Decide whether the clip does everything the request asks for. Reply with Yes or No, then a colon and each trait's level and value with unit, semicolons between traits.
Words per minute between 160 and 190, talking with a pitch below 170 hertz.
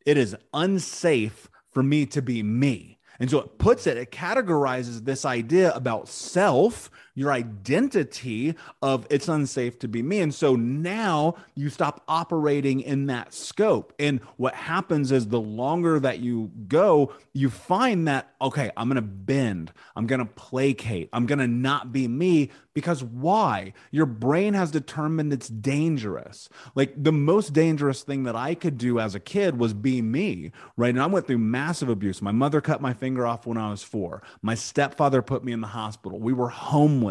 Yes: average, 185 wpm; low, 135 Hz